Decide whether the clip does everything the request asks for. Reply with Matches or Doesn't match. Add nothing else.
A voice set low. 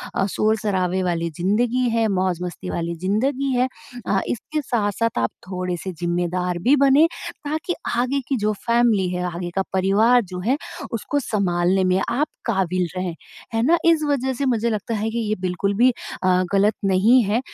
Doesn't match